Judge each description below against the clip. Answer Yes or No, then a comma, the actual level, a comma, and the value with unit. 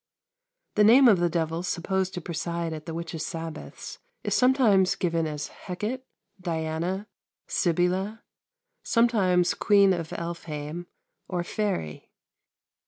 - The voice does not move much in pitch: No, average, 3.3 semitones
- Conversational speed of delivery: No, slow, 115 wpm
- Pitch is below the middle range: No, medium, 175 Hz